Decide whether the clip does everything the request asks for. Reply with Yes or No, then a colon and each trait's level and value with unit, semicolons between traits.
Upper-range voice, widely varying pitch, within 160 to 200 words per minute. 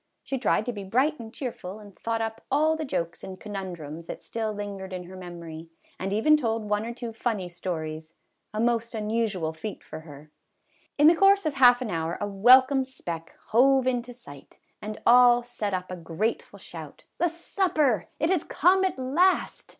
Yes: high, 220 Hz; wide, 6.0 semitones; average, 195 wpm